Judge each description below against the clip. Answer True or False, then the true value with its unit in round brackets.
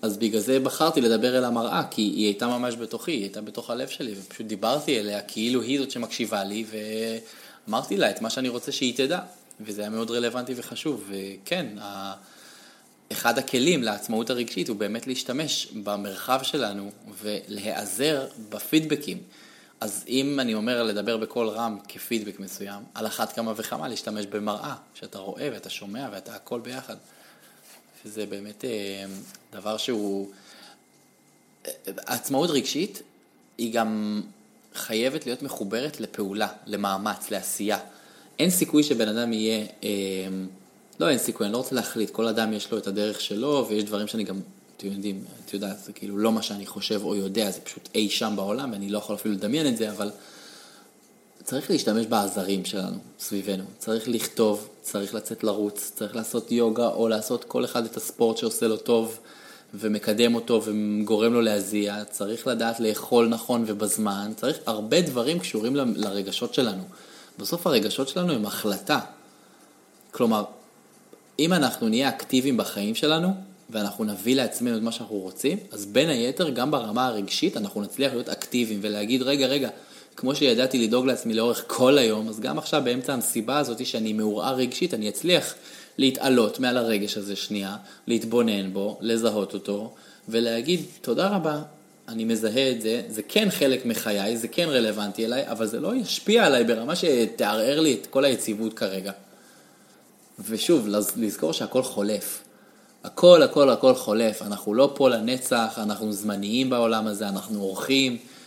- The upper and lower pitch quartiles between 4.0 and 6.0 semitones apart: False (2.7 semitones)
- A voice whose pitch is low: True (110 Hz)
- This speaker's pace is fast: True (155 wpm)